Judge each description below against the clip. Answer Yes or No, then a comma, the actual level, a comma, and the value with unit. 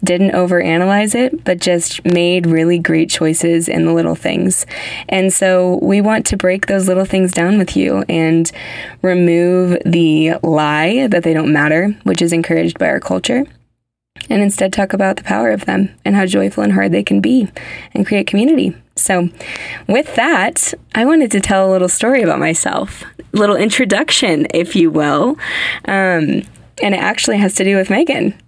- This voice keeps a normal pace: Yes, average, 180 wpm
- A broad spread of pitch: No, average, 3.3 semitones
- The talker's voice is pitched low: No, medium, 180 Hz